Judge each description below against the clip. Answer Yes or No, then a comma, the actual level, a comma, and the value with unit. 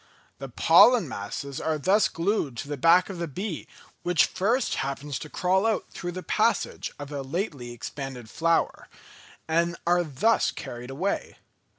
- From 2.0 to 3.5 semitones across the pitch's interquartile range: No, average, 5.0 semitones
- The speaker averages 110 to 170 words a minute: Yes, average, 160 wpm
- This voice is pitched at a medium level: Yes, medium, 165 Hz